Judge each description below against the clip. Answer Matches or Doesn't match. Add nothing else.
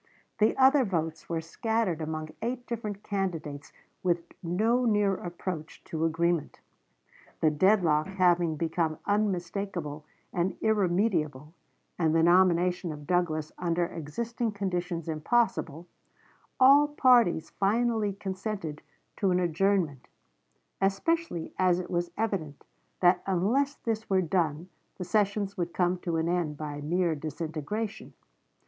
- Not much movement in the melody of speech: Doesn't match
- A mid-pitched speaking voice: Matches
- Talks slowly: Matches